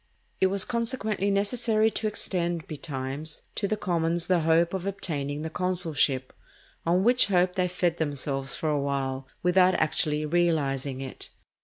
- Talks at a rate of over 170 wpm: No, average, 150 wpm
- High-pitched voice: No, medium, 170 Hz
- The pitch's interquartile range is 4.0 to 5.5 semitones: Yes, average, 4.5 semitones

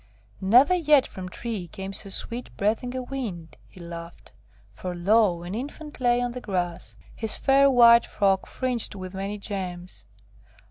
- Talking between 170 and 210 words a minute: No, average, 155 wpm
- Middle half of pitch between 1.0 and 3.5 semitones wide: No, average, 5.1 semitones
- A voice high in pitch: Yes, high, 210 Hz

